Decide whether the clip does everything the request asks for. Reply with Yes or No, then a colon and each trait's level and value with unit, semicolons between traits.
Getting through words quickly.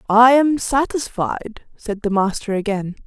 No: slow, 135 wpm